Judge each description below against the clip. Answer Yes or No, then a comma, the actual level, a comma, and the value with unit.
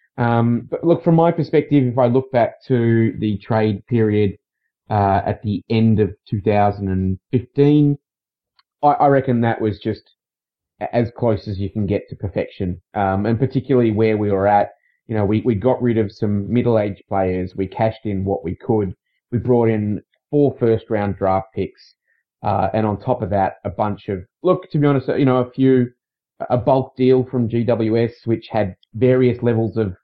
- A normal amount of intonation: Yes, average, 3.6 semitones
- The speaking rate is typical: Yes, average, 180 wpm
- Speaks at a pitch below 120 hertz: Yes, low, 110 Hz